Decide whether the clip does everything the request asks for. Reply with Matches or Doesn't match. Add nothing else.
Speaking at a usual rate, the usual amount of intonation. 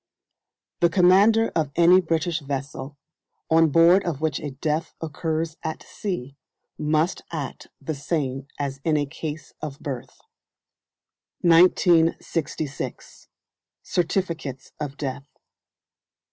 Doesn't match